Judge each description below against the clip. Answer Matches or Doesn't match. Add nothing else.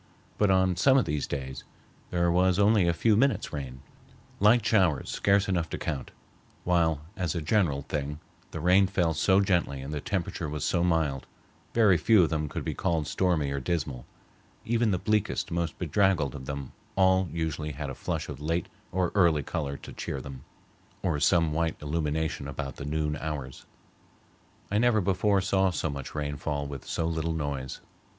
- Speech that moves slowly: Doesn't match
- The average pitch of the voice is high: Doesn't match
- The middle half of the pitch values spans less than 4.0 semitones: Doesn't match